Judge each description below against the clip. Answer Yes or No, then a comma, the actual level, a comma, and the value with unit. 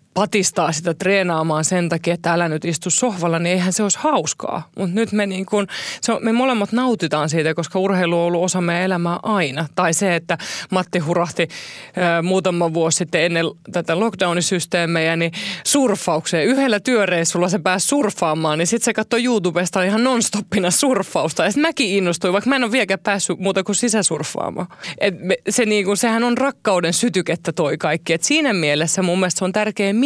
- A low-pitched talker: No, medium, 185 Hz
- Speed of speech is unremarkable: No, fast, 185 wpm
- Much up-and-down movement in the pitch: No, average, 3.7 semitones